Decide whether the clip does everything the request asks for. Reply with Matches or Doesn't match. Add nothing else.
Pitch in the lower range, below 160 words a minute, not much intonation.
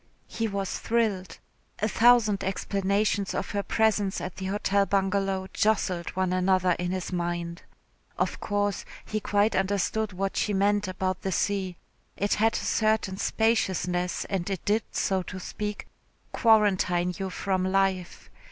Doesn't match